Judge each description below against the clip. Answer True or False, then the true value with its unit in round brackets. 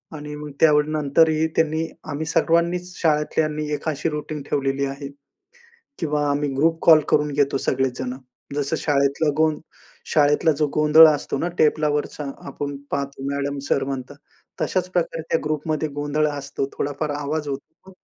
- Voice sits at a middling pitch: True (150 Hz)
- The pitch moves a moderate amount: False (1.8 semitones)